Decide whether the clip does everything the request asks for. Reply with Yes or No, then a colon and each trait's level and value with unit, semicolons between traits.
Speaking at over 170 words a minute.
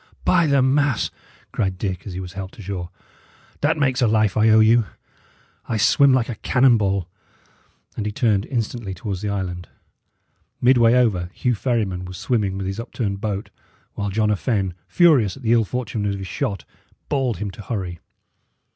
Yes: average, 180 wpm